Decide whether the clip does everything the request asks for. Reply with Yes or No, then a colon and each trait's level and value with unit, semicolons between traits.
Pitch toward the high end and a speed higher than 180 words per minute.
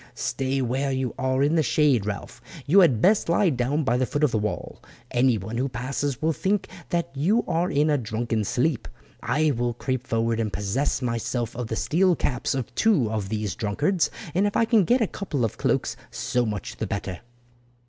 No: low, 130 Hz; average, 200 wpm